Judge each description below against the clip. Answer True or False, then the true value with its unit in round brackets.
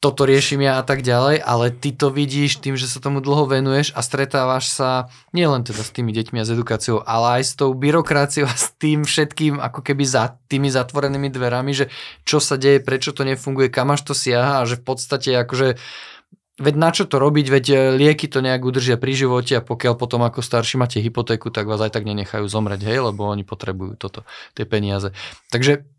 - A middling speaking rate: False (210 wpm)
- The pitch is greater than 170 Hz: False (130 Hz)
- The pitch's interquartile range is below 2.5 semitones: False (2.8 semitones)